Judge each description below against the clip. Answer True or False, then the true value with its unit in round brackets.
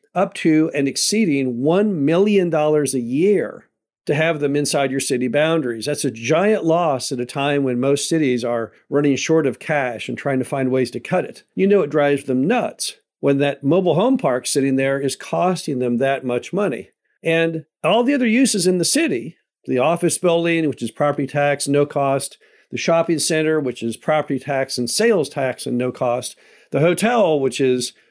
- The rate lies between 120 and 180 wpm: False (195 wpm)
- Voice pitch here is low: False (145 Hz)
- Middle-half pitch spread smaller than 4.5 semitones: True (3.9 semitones)